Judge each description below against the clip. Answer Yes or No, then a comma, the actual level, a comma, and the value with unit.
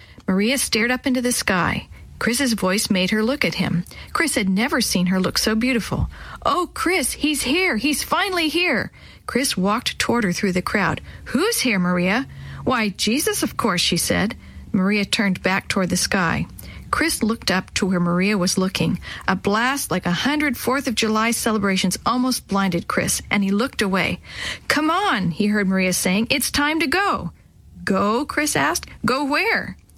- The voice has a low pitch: No, high, 225 Hz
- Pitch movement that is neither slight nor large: No, wide, 6.3 semitones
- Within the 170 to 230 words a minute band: Yes, average, 180 wpm